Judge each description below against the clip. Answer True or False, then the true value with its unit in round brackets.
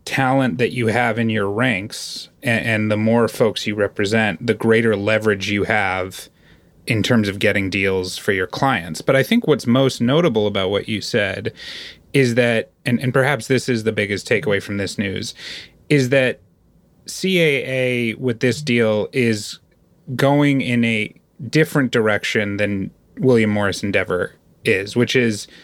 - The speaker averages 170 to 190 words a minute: False (160 wpm)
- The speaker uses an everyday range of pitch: True (3.7 semitones)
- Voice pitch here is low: True (115 Hz)